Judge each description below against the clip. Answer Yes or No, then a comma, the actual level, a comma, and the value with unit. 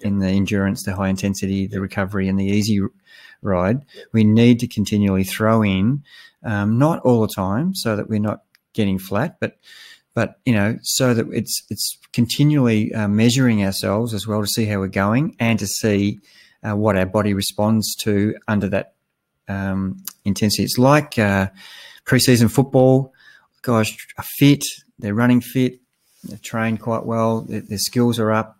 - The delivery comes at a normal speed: Yes, average, 165 wpm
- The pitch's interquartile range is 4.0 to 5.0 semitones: No, average, 3.2 semitones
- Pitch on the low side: Yes, low, 110 Hz